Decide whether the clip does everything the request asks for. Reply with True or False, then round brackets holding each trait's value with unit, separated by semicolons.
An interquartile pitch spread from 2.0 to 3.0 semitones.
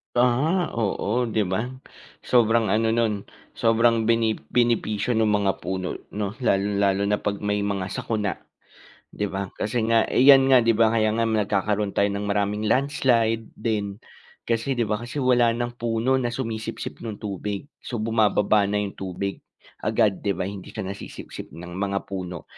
True (2.5 semitones)